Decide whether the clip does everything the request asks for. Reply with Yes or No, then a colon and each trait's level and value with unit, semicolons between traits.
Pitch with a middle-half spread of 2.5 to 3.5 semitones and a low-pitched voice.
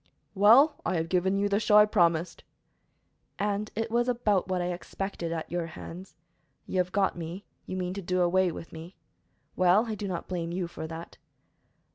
No: average, 2.8 semitones; medium, 185 Hz